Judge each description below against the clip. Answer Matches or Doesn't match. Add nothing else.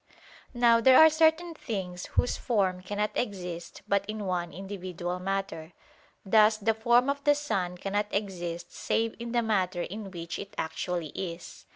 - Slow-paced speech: Doesn't match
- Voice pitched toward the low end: Doesn't match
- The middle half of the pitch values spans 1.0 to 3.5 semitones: Doesn't match